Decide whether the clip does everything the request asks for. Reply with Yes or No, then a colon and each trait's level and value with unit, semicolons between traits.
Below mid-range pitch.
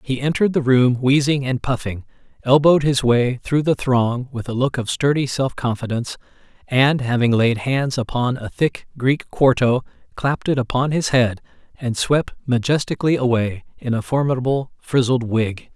Yes: low, 130 Hz